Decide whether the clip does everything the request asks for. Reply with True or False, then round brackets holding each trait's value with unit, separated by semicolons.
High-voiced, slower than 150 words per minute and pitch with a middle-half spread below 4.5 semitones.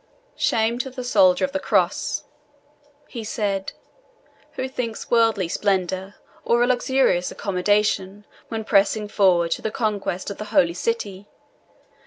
True (210 Hz; 140 wpm; 3.5 semitones)